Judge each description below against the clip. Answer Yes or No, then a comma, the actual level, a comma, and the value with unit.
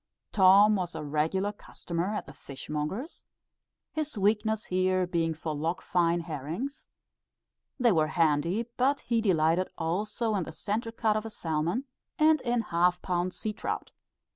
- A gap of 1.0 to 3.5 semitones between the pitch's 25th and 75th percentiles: No, average, 4.9 semitones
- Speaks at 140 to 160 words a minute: Yes, average, 155 wpm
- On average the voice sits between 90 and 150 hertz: No, medium, 185 Hz